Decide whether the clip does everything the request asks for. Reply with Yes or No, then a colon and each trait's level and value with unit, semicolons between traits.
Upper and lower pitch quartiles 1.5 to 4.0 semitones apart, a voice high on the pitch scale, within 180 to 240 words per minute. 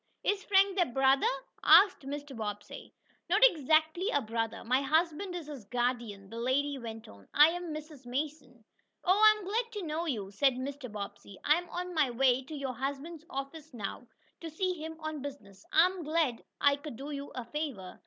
No: average, 4.9 semitones; very high, 285 Hz; average, 195 wpm